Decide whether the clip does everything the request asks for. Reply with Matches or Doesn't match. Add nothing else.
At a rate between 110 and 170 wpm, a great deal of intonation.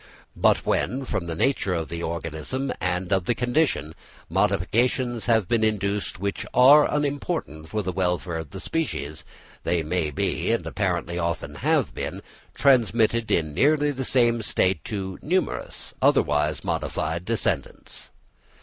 Matches